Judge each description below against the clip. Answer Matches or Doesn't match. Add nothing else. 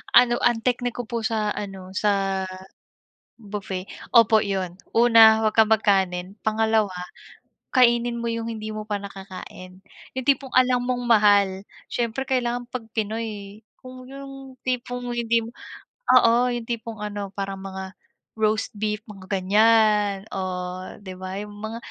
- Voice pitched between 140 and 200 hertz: Doesn't match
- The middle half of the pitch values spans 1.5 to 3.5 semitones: Matches